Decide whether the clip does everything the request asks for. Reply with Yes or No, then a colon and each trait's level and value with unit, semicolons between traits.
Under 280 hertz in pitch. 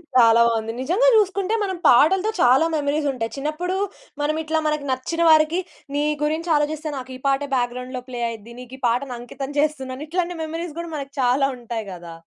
No: very high, 285 Hz